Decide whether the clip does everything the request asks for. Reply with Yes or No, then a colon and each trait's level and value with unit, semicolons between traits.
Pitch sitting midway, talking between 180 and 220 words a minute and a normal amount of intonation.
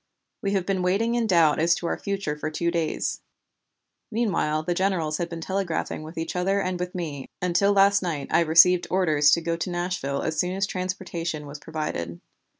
Yes: medium, 175 Hz; average, 195 wpm; average, 3.2 semitones